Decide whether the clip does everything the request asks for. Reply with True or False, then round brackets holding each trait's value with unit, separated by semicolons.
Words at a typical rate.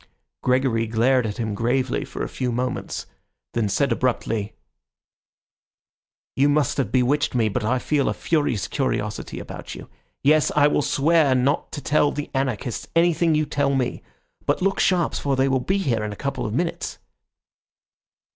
True (170 wpm)